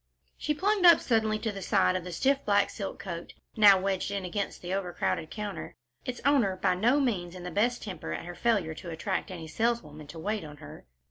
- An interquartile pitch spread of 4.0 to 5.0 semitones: Yes, average, 4.3 semitones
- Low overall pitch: No, high, 195 Hz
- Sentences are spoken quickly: Yes, fast, 215 wpm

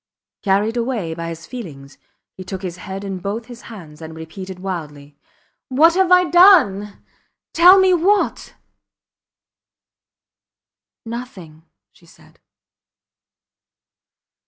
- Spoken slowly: Yes, slow, 110 wpm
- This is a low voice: No, high, 200 Hz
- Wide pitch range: Yes, wide, 7.5 semitones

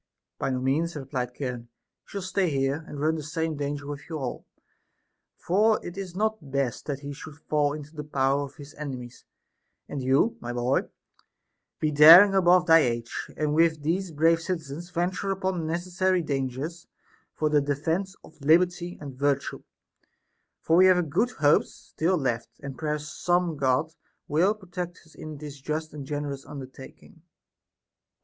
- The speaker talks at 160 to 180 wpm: Yes, average, 170 wpm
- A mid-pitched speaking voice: Yes, medium, 150 Hz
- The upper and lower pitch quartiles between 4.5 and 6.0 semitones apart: No, average, 3.8 semitones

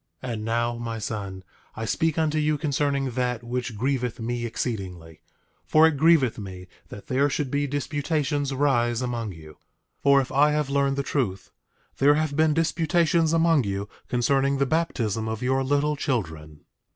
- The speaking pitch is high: No, low, 135 Hz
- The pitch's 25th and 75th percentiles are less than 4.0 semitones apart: No, average, 4.3 semitones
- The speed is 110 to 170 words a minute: Yes, average, 165 wpm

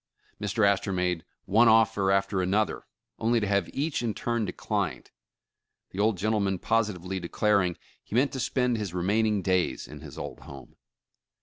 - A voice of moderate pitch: No, low, 100 Hz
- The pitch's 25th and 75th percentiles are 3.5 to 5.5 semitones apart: No, average, 3.1 semitones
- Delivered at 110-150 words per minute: No, average, 165 wpm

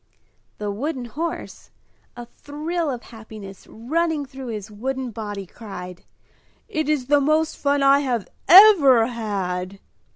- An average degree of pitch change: No, wide, 5.7 semitones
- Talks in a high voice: Yes, very high, 250 Hz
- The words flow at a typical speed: No, slow, 130 wpm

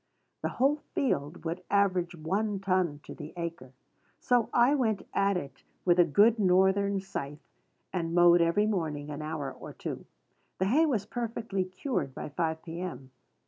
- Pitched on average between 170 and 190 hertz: Yes, medium, 185 Hz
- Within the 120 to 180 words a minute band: Yes, average, 160 wpm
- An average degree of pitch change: Yes, average, 4.2 semitones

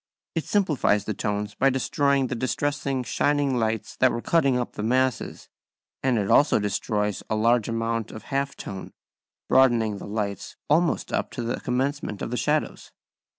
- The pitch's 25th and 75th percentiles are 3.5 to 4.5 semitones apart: Yes, average, 4.1 semitones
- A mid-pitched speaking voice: No, low, 125 Hz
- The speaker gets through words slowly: No, average, 165 wpm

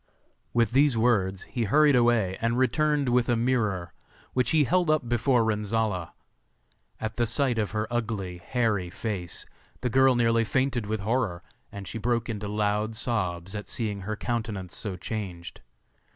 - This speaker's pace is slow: No, average, 160 wpm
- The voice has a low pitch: Yes, low, 115 Hz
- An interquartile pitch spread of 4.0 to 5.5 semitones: No, average, 3.1 semitones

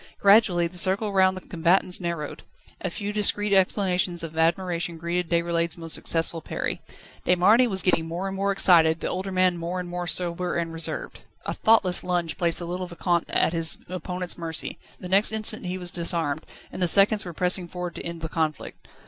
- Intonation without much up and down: Yes, narrow, 1.9 semitones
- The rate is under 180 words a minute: No, average, 195 wpm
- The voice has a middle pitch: Yes, medium, 180 Hz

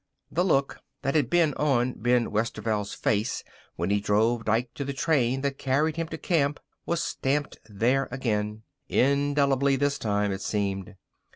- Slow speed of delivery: No, average, 160 wpm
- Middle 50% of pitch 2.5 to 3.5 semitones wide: No, average, 4.7 semitones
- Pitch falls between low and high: No, low, 130 Hz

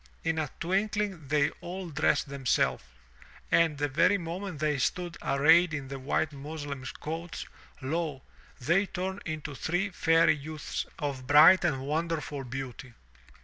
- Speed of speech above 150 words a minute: No, average, 140 wpm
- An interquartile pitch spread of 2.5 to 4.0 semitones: Yes, average, 3.6 semitones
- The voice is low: No, medium, 155 Hz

